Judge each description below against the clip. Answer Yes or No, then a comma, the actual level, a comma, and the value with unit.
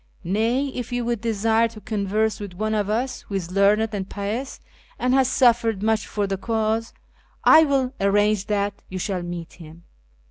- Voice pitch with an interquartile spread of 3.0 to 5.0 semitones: No, narrow, 2.6 semitones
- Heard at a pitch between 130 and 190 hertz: No, high, 215 Hz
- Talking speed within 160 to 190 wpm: Yes, average, 180 wpm